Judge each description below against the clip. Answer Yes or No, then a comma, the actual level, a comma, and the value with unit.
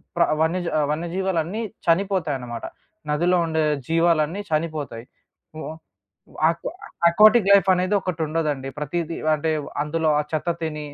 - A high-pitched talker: No, medium, 165 Hz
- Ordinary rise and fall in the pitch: Yes, average, 3.1 semitones